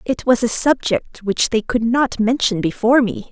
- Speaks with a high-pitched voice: Yes, high, 235 Hz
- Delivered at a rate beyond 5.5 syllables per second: No, 4.7 syllables/s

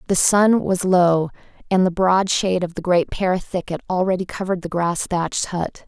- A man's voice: No, female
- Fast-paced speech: No, average, 195 wpm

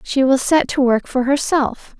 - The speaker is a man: No, female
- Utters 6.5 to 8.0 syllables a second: No, 4.2 syllables/s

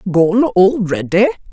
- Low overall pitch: No, high, 200 Hz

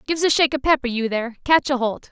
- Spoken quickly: Yes, fast, 255 wpm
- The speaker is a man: No, female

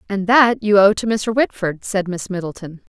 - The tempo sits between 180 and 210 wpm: Yes, fast, 205 wpm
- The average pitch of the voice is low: No, high, 200 Hz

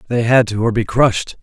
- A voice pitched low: Yes, low, 115 Hz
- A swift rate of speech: Yes, fast, 255 wpm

